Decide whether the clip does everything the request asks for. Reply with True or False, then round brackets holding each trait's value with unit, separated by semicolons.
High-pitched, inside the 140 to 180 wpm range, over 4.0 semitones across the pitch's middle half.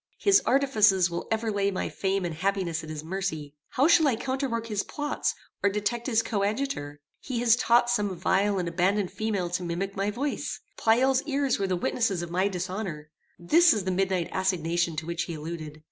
False (195 Hz; 190 wpm; 5.1 semitones)